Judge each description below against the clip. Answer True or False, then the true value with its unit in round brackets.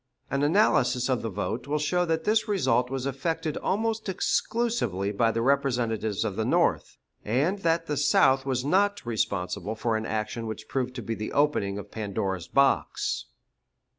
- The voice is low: True (130 Hz)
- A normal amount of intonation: False (6.5 semitones)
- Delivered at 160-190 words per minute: True (165 wpm)